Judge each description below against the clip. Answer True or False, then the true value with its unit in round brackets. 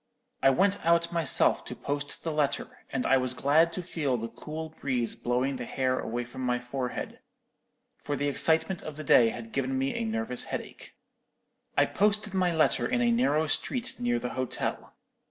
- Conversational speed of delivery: True (185 wpm)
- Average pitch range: True (5.0 semitones)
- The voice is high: False (140 Hz)